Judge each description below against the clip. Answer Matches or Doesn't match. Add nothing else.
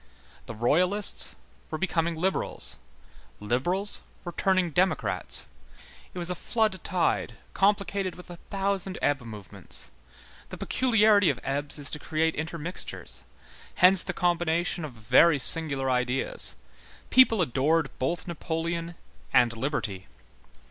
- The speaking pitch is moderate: Matches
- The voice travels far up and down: Doesn't match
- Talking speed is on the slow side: Matches